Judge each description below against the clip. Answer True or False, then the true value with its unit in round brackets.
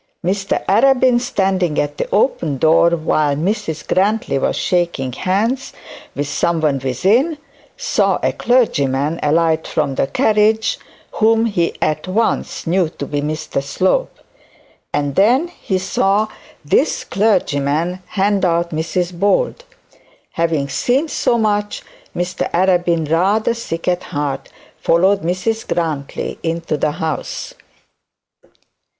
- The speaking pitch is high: False (175 Hz)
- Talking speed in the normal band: False (120 wpm)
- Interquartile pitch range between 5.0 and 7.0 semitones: True (5.4 semitones)